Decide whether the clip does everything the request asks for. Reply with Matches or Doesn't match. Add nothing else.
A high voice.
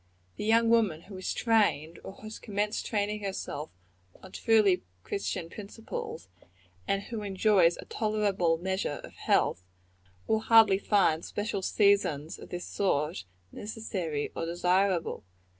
Matches